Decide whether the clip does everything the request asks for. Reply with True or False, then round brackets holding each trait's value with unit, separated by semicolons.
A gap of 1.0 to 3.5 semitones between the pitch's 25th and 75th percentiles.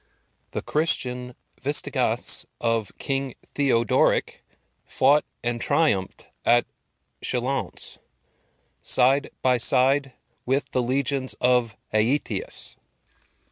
True (2.4 semitones)